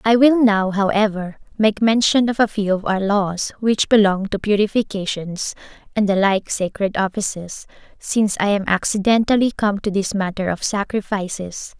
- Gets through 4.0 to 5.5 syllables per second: Yes, 4.8 syllables/s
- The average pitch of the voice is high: Yes, high, 205 Hz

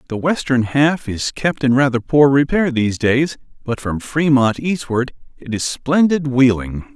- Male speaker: Yes, male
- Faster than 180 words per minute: No, average, 165 wpm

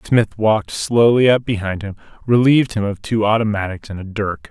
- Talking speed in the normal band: Yes, average, 185 wpm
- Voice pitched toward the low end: Yes, low, 105 Hz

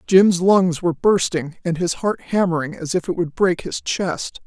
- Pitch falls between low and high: Yes, medium, 175 Hz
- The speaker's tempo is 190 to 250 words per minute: Yes, average, 200 wpm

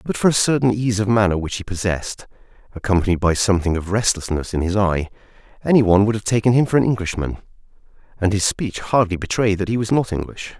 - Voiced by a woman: No, male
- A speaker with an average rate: No, fast, 210 wpm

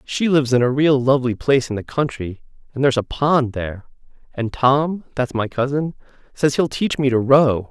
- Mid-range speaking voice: No, low, 130 Hz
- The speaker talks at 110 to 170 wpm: No, average, 200 wpm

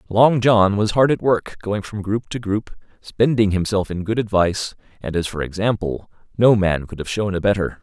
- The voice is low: Yes, low, 100 Hz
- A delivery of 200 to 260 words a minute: Yes, fast, 205 wpm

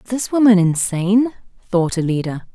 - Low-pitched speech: No, high, 200 Hz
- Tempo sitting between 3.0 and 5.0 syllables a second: No, 5.4 syllables/s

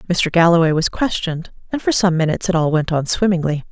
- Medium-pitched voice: Yes, medium, 170 Hz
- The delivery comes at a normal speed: No, fast, 210 wpm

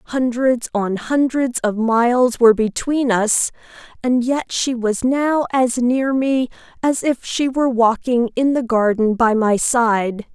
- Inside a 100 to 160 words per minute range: Yes, average, 150 wpm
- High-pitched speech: Yes, high, 245 Hz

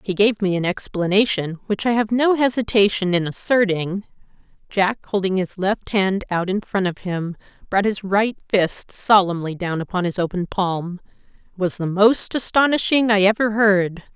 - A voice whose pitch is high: Yes, high, 200 Hz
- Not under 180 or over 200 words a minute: No, average, 155 wpm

